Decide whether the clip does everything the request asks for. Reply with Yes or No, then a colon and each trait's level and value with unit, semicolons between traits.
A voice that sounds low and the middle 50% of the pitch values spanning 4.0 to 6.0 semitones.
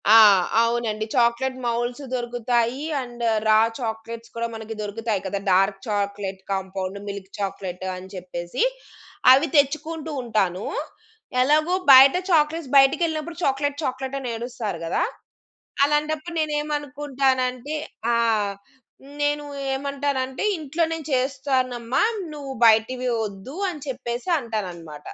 No: very high, 250 Hz; average, 4.8 semitones